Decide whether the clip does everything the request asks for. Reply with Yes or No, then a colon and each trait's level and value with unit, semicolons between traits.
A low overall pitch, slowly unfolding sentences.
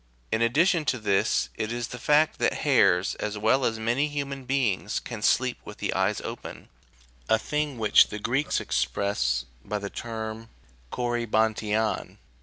No: low, 110 Hz; average, 155 wpm